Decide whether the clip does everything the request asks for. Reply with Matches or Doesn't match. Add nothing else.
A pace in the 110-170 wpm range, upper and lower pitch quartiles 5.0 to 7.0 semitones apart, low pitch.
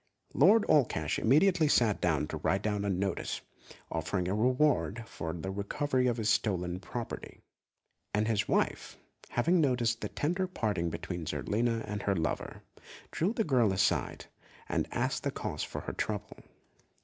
Matches